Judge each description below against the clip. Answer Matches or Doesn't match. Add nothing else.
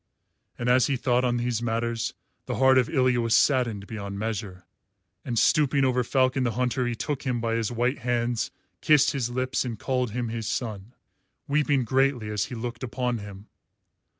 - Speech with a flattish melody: Matches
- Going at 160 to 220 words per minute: Matches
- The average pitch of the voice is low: Matches